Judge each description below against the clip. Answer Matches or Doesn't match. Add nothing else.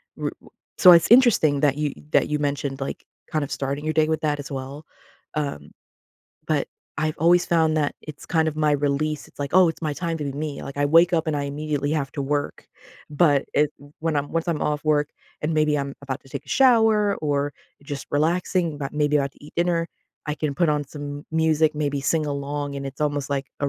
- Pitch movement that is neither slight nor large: Doesn't match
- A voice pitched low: Doesn't match